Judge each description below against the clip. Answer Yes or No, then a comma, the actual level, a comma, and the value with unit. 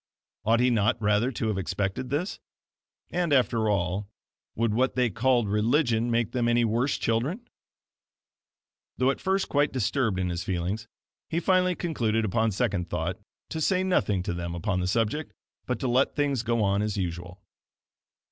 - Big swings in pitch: No, average, 4.6 semitones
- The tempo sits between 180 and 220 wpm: No, average, 165 wpm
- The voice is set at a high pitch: No, low, 115 Hz